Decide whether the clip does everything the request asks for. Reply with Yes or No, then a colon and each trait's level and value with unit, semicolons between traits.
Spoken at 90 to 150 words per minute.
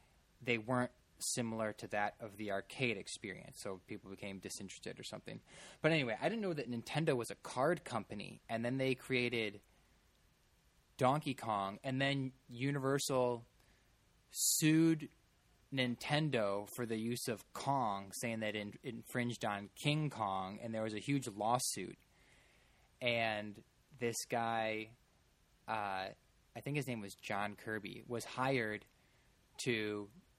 Yes: slow, 135 wpm